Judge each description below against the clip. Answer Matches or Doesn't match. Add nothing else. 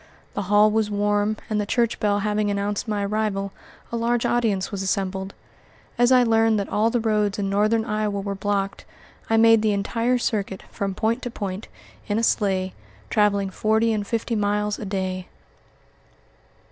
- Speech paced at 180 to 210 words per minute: Doesn't match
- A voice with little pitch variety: Matches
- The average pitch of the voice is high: Matches